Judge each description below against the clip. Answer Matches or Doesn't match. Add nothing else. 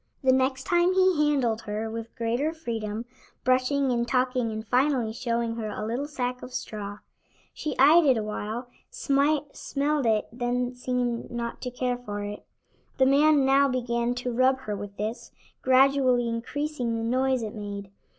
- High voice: Matches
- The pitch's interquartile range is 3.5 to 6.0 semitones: Doesn't match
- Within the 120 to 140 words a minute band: Doesn't match